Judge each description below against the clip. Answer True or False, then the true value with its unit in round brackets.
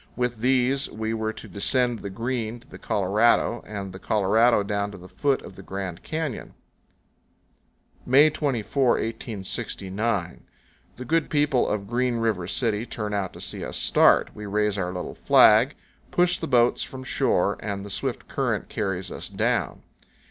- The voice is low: True (110 Hz)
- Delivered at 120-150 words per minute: False (165 wpm)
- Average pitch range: True (3.9 semitones)